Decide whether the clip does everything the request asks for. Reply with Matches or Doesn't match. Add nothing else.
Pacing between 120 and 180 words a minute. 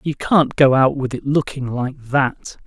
Doesn't match